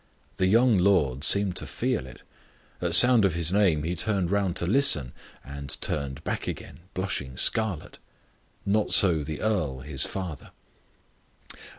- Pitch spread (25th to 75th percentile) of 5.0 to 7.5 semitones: Yes, wide, 5.5 semitones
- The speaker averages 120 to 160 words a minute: Yes, average, 150 wpm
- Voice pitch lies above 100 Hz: No, very low, 90 Hz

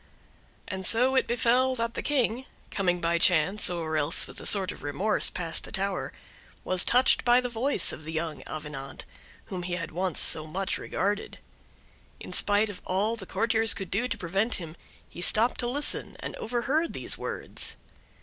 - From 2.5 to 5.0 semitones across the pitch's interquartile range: No, wide, 5.4 semitones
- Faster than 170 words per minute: Yes, average, 180 wpm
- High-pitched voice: Yes, high, 195 Hz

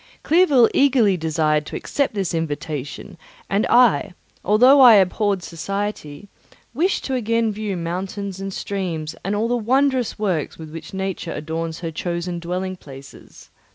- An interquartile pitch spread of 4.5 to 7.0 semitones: Yes, wide, 5.4 semitones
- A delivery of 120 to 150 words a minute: Yes, average, 145 wpm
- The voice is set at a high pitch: Yes, high, 195 Hz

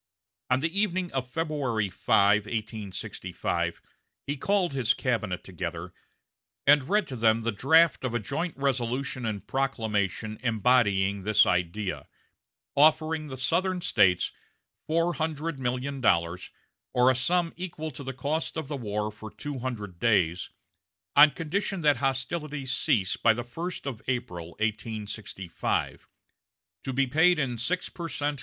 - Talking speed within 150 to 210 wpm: No, average, 140 wpm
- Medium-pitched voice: No, low, 130 Hz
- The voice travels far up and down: Yes, wide, 6.0 semitones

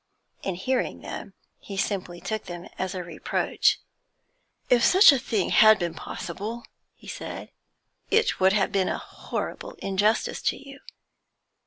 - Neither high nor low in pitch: No, high, 200 Hz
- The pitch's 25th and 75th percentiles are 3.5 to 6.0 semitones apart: Yes, average, 4.1 semitones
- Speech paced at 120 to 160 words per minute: Yes, average, 145 wpm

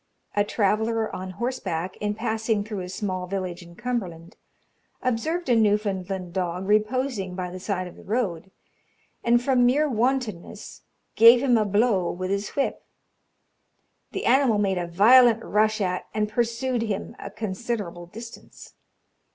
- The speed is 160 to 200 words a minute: No, average, 145 wpm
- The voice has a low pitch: No, high, 210 Hz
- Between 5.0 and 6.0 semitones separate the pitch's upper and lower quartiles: No, average, 4.2 semitones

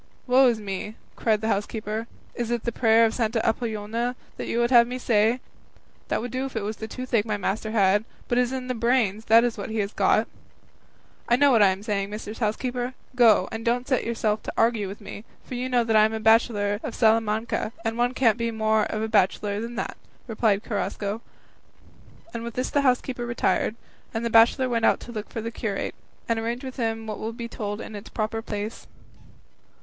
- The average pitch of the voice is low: No, high, 225 Hz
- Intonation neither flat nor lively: No, narrow, 1.9 semitones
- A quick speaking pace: Yes, fast, 210 wpm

